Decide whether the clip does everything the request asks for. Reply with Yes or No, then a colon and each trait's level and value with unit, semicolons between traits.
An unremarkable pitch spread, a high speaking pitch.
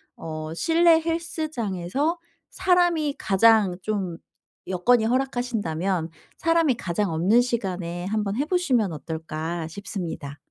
No: wide, 8.3 semitones; high, 210 Hz